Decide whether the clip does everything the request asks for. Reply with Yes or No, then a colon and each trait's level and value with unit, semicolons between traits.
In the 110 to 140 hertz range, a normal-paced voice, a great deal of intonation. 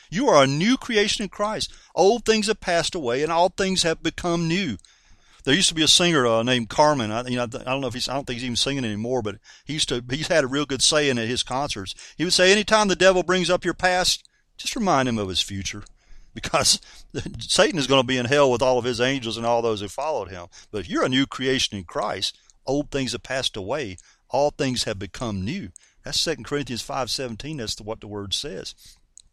No: low, 135 Hz; fast, 245 wpm; wide, 6.1 semitones